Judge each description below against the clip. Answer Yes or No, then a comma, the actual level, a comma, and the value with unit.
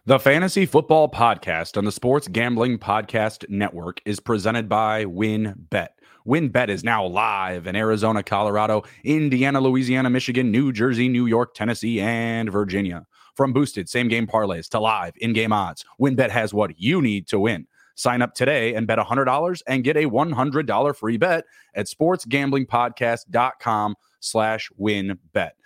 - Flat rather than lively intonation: No, average, 3.7 semitones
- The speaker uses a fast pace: No, average, 160 wpm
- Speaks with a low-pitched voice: Yes, low, 115 Hz